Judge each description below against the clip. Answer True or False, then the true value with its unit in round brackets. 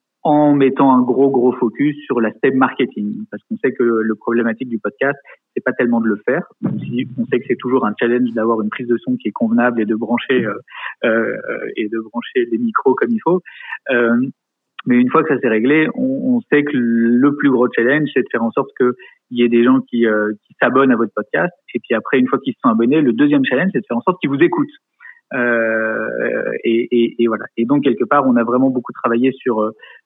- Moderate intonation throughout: True (3.9 semitones)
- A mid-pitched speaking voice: False (125 Hz)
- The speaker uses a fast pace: True (245 wpm)